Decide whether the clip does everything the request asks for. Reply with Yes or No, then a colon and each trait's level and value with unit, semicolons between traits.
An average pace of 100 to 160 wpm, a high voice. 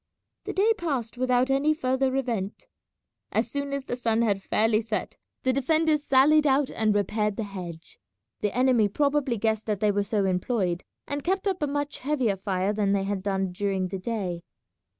No: average, 185 wpm; high, 225 Hz